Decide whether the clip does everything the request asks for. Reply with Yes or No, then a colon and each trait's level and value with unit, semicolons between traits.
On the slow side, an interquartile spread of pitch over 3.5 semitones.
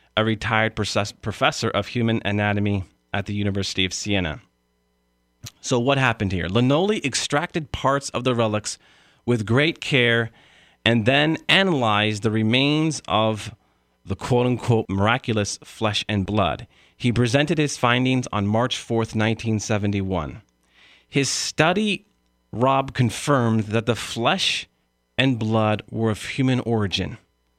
Yes: slow, 130 wpm; average, 4.1 semitones